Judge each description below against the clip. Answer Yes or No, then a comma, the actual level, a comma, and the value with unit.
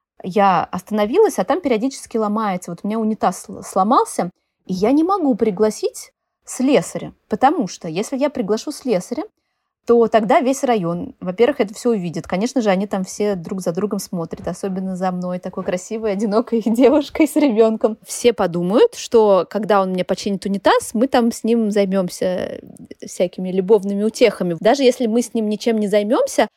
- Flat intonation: No, average, 4.2 semitones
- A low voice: No, high, 220 Hz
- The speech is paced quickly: Yes, fast, 165 wpm